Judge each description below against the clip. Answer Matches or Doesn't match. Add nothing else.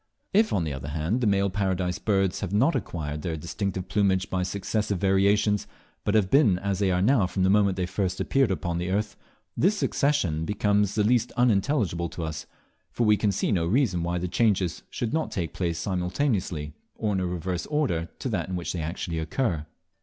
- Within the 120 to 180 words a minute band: Doesn't match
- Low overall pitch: Matches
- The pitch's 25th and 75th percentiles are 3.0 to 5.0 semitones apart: Matches